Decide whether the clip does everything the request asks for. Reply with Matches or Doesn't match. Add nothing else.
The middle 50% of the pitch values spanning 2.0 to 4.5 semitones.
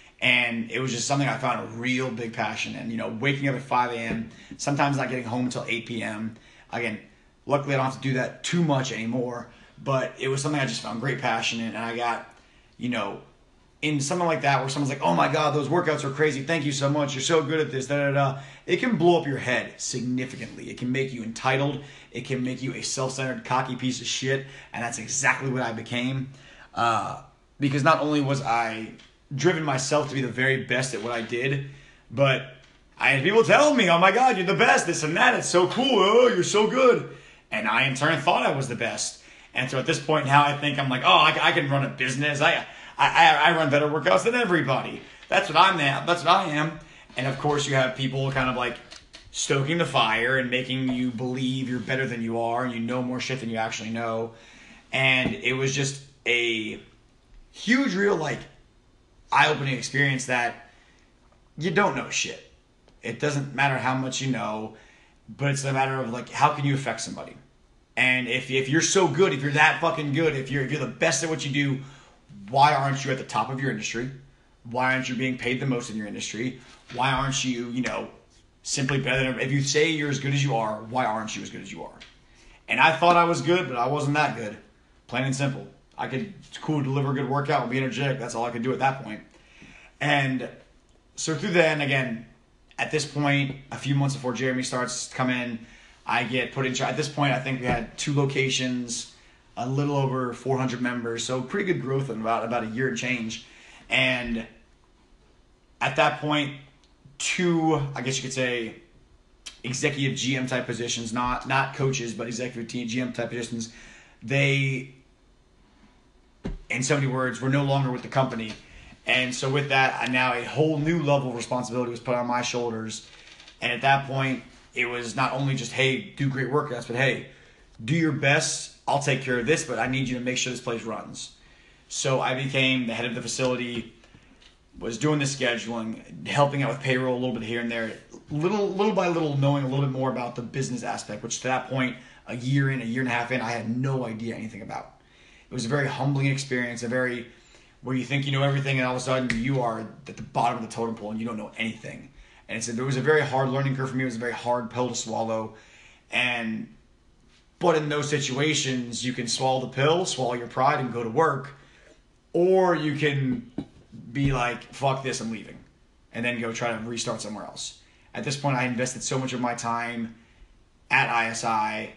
Matches